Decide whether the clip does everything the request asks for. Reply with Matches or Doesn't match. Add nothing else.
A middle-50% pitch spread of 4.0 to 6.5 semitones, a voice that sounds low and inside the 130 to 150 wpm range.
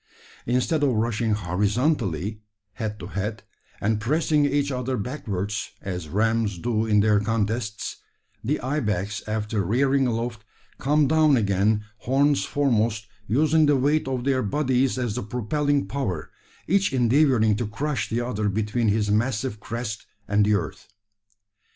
Matches